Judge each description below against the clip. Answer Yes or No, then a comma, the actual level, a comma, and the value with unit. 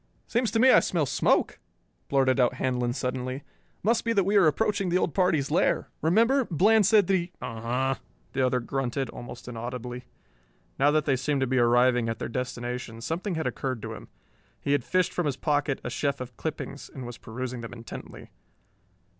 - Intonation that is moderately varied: No, wide, 6.1 semitones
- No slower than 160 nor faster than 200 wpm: Yes, average, 195 wpm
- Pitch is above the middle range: No, low, 135 Hz